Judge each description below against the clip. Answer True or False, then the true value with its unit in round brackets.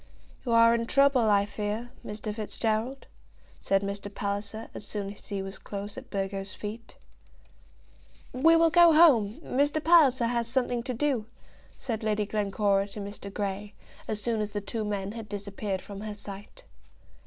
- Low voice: False (215 Hz)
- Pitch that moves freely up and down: False (3.0 semitones)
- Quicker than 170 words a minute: False (165 wpm)